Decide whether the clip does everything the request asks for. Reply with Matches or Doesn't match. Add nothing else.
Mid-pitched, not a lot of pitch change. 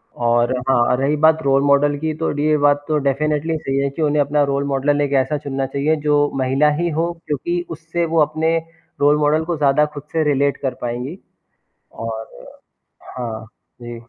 Matches